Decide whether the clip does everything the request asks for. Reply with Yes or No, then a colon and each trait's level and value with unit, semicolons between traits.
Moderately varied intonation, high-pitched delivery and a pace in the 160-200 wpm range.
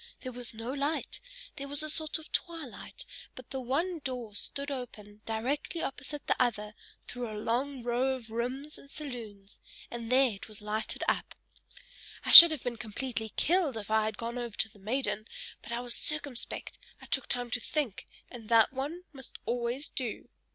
Yes: average, 3.7 semitones; high, 245 Hz; average, 185 wpm